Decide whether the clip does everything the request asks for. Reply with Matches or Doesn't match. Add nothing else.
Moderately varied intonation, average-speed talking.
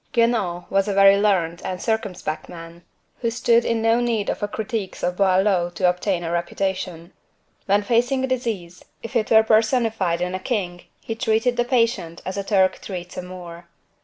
Matches